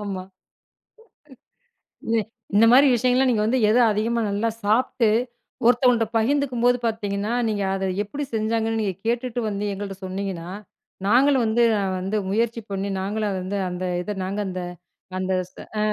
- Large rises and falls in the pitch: No, average, 3.1 semitones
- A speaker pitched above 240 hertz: No, high, 220 Hz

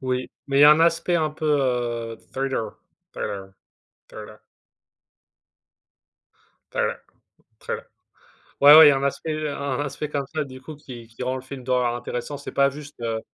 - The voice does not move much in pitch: No, average, 3.2 semitones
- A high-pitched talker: No, low, 135 Hz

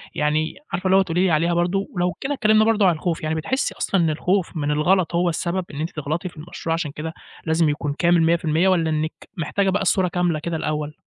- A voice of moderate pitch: Yes, medium, 170 Hz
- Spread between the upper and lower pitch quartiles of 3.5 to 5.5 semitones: No, average, 2.9 semitones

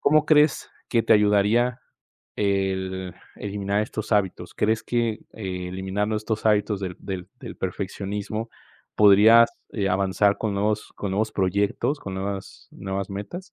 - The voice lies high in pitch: No, low, 100 Hz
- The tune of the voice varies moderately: No, narrow, 2.2 semitones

